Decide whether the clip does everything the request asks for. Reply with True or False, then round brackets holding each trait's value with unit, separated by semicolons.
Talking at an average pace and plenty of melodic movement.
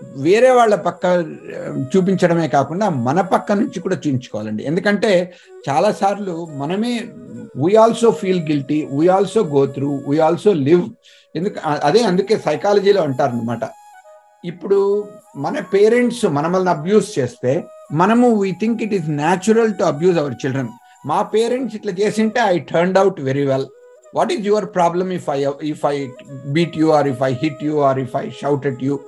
False (155 wpm; 6.3 semitones)